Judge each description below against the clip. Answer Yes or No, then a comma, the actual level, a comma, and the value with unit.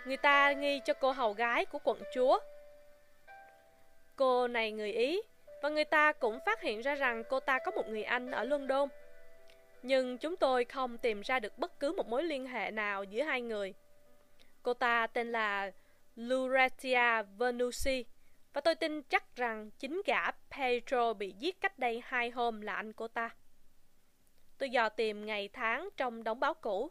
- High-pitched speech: Yes, high, 245 Hz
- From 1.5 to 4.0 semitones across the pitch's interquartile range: No, average, 4.8 semitones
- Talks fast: No, average, 180 wpm